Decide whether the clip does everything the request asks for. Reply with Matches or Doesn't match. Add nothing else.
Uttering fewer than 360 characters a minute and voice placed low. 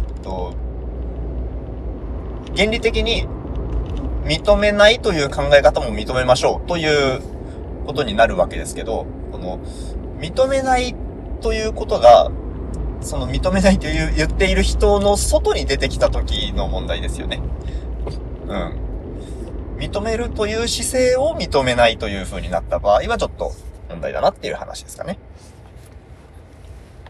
Matches